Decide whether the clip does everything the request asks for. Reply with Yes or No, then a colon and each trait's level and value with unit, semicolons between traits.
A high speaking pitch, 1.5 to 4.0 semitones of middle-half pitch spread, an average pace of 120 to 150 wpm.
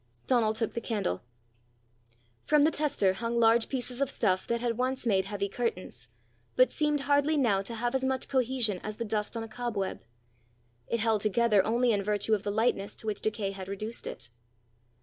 No: high, 225 Hz; average, 3.3 semitones; average, 190 wpm